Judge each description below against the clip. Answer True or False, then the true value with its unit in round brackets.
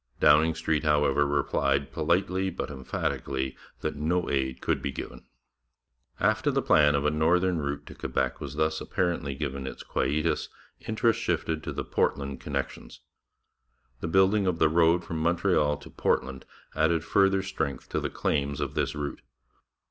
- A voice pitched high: False (75 Hz)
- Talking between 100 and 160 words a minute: True (155 wpm)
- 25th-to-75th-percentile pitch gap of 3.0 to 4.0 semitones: True (3.3 semitones)